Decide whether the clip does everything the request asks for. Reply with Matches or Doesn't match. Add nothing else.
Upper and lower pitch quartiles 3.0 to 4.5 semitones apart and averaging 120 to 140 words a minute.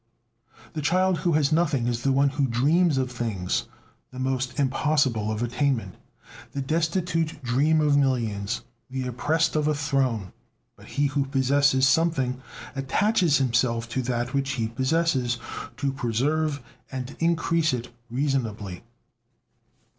Matches